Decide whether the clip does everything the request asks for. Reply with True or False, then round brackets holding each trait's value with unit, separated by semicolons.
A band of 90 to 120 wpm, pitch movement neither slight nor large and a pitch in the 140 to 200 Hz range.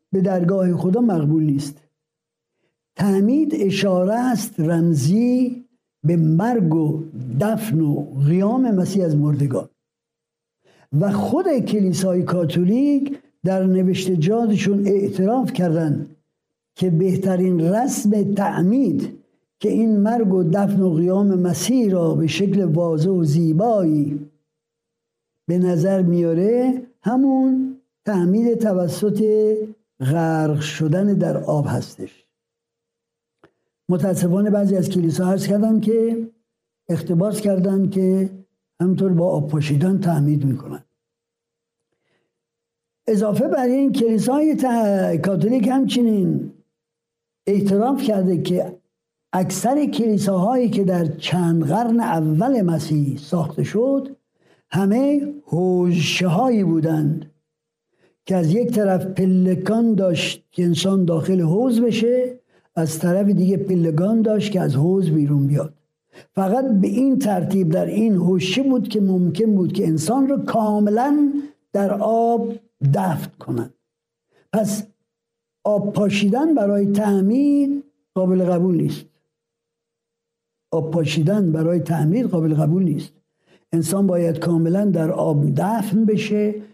True (110 wpm; 4.9 semitones; 190 Hz)